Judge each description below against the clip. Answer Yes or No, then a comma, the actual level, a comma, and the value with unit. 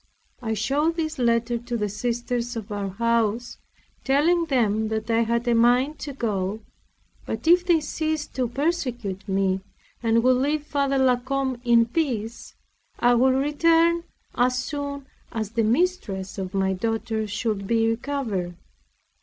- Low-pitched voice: No, high, 240 Hz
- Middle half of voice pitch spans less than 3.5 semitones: No, average, 4.3 semitones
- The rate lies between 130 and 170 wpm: Yes, average, 150 wpm